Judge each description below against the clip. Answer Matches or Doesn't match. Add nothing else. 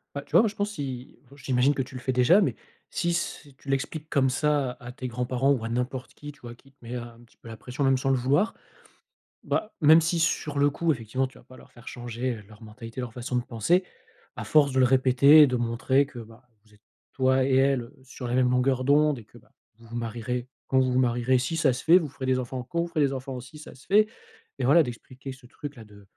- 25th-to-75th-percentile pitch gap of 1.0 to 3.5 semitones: Matches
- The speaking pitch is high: Doesn't match